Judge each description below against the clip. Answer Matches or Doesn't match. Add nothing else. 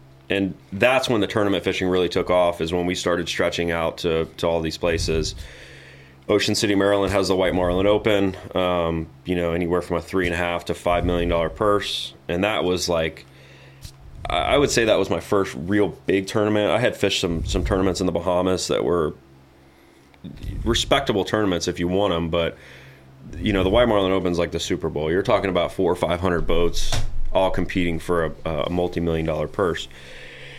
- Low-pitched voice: Matches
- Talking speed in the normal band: Matches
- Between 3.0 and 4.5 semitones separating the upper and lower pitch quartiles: Doesn't match